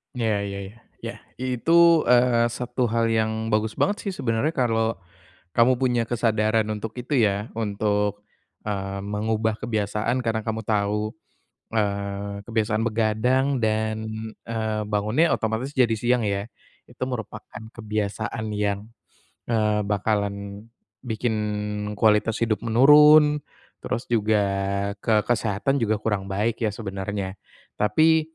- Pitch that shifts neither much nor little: No, narrow, 2.2 semitones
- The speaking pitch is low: Yes, low, 110 Hz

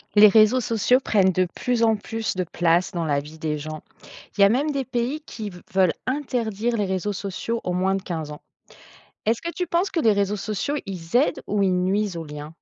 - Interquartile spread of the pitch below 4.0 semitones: No, average, 4.7 semitones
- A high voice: Yes, high, 205 Hz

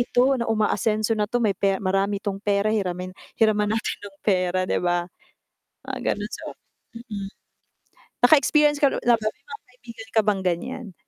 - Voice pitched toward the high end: Yes, high, 210 Hz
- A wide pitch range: No, average, 3.2 semitones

